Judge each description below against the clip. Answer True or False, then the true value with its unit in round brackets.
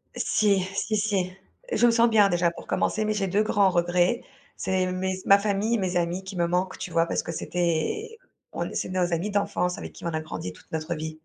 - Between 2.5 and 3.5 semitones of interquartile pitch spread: True (2.9 semitones)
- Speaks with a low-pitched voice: False (185 Hz)